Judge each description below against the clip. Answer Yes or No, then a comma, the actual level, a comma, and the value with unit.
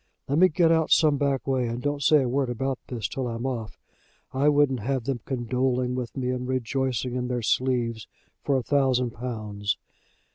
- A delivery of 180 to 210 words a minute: Yes, average, 190 wpm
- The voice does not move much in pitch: Yes, narrow, 2.1 semitones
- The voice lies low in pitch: Yes, low, 130 Hz